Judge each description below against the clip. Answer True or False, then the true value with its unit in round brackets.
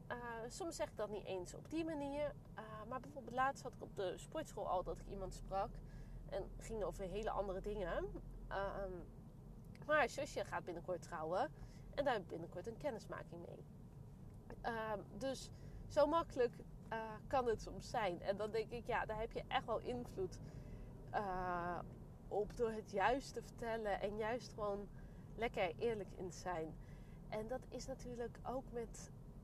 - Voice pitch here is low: False (205 Hz)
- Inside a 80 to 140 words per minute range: False (175 wpm)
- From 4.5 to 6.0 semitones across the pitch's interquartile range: True (5.1 semitones)